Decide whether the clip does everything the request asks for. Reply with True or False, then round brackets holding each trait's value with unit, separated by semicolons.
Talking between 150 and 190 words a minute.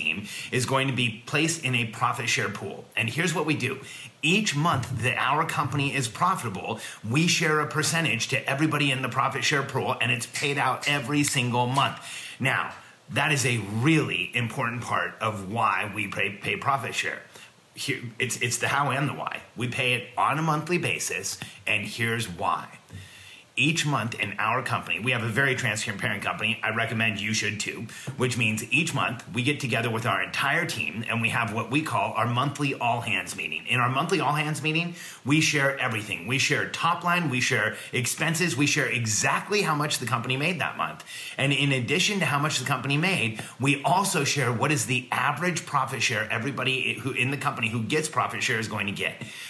False (200 wpm)